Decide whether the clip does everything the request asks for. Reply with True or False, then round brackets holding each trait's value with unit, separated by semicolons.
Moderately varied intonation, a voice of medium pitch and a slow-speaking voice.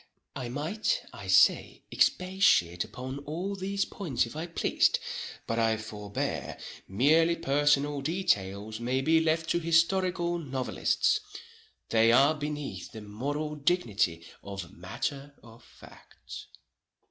False (6.6 semitones; 145 Hz; 110 wpm)